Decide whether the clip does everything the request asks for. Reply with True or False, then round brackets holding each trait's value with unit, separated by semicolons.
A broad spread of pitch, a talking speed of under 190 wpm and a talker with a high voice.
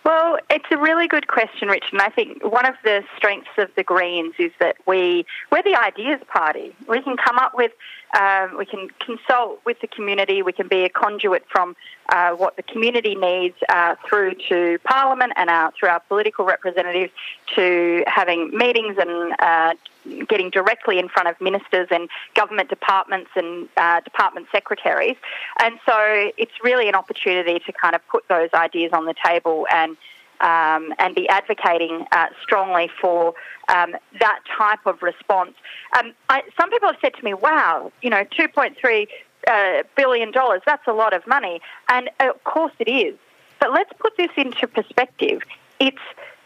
True (6.9 semitones; 175 wpm; 210 Hz)